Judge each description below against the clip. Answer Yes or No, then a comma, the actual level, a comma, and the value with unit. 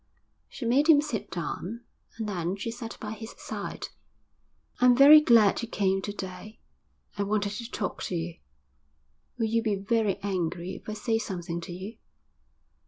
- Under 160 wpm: No, average, 170 wpm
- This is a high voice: Yes, high, 210 Hz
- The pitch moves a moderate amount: Yes, average, 3.5 semitones